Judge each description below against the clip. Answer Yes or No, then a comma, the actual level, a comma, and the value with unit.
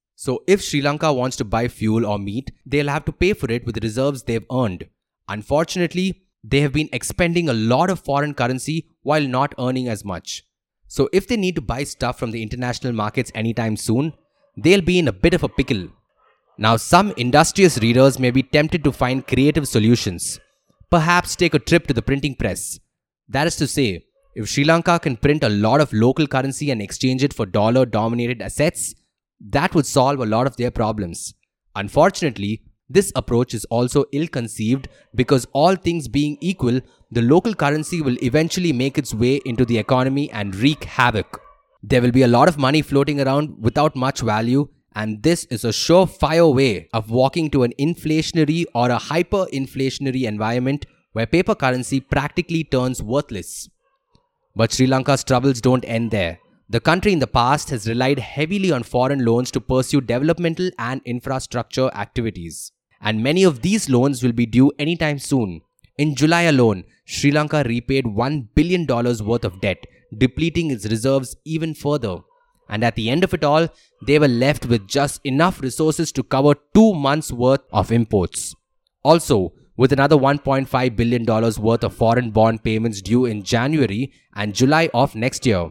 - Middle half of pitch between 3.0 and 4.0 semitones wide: No, average, 4.4 semitones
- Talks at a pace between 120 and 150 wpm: No, average, 175 wpm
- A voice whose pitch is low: Yes, low, 130 Hz